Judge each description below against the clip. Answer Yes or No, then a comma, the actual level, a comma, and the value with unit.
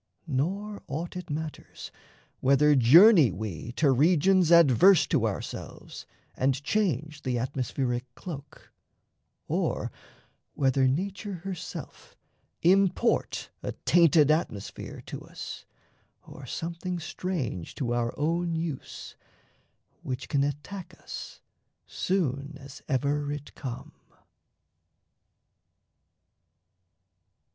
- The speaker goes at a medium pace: No, slow, 95 wpm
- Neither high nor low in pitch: Yes, medium, 150 Hz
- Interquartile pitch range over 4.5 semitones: Yes, average, 4.9 semitones